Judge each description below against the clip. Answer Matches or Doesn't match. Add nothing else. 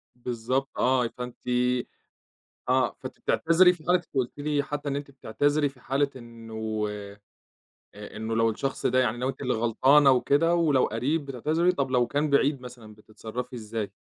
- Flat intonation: Doesn't match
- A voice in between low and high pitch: Doesn't match